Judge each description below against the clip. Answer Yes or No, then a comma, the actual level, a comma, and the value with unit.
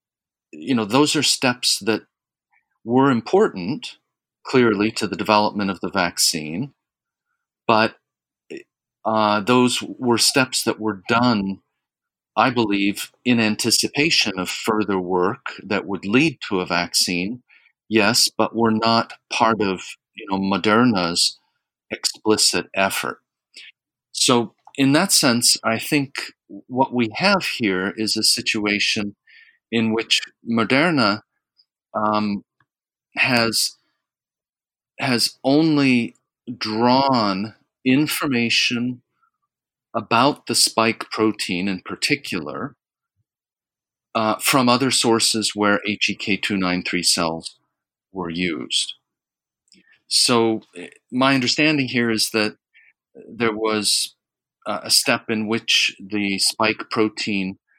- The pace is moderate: No, slow, 105 wpm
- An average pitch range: Yes, average, 3.3 semitones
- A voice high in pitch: No, low, 110 Hz